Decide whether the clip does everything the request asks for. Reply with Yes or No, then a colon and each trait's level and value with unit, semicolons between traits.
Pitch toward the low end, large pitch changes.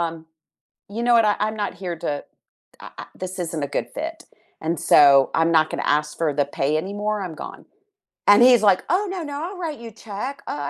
No: high, 190 Hz; wide, 7.0 semitones